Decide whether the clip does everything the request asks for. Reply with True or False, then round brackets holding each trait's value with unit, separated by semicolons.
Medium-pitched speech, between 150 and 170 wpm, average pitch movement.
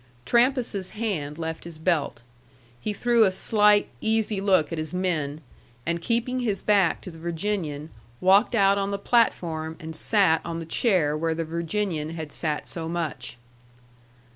True (175 Hz; 160 wpm; 4.5 semitones)